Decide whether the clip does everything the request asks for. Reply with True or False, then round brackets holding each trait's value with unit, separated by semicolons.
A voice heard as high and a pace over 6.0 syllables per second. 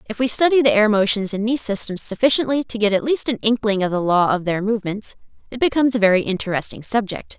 True (215 Hz; 6.5 syllables/s)